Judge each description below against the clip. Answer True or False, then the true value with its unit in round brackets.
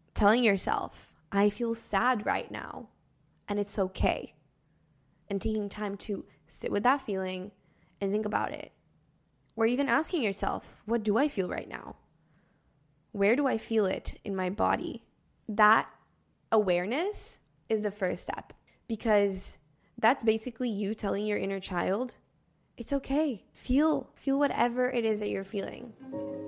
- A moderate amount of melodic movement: True (3.5 semitones)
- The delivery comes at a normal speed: True (145 wpm)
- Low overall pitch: False (210 Hz)